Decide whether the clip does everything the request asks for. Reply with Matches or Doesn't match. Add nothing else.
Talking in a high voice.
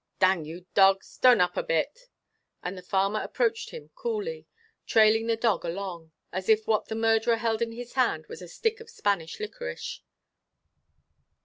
Matches